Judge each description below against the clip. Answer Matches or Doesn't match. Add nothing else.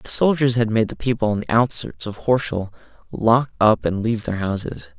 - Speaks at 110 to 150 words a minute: Doesn't match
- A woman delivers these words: Doesn't match